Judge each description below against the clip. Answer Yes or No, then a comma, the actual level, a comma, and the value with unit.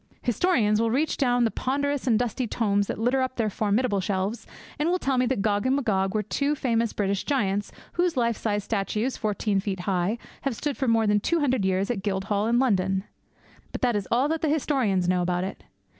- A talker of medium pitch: No, high, 225 Hz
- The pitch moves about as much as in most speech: Yes, average, 4.6 semitones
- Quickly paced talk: Yes, fast, 220 wpm